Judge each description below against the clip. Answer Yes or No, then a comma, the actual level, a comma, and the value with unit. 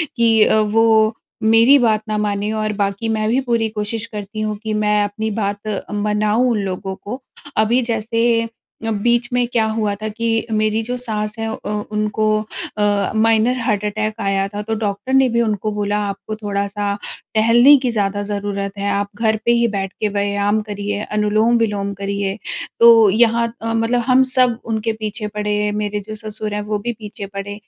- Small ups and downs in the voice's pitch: Yes, narrow, 1.7 semitones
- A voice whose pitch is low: No, high, 215 Hz